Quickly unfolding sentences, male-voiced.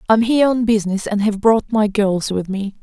No: fast, 235 wpm; female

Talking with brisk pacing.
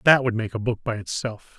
Yes: fast, 265 wpm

